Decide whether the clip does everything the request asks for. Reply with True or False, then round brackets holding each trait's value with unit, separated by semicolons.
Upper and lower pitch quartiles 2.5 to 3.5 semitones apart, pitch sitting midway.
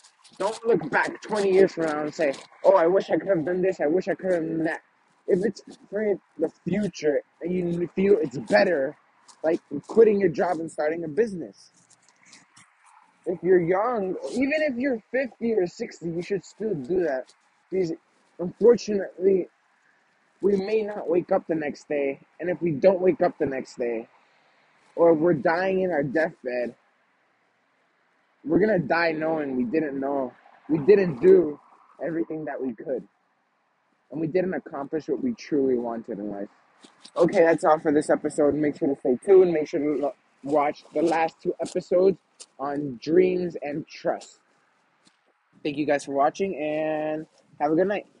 False (4.1 semitones; 170 Hz)